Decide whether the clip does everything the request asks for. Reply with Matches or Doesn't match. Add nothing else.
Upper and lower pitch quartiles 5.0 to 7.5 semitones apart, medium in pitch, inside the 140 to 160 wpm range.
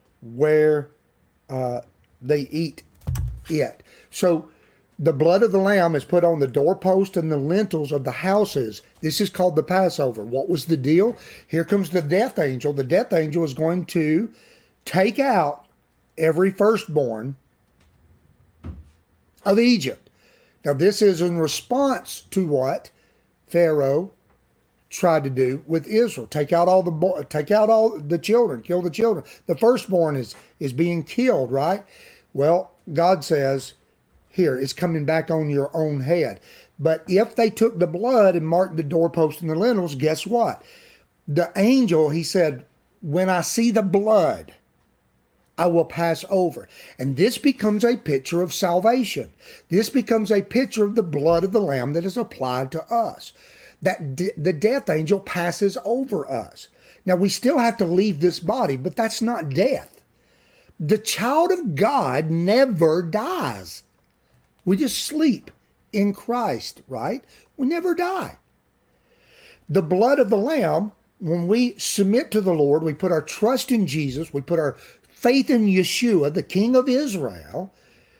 Matches